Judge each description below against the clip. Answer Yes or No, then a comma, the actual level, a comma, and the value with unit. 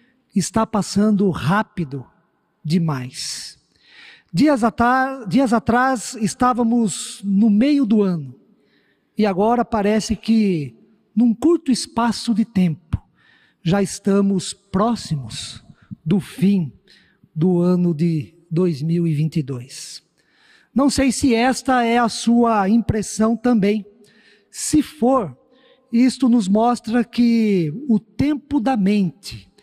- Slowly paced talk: Yes, slow, 100 wpm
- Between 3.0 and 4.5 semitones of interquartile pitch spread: No, average, 5.2 semitones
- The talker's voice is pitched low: No, high, 215 Hz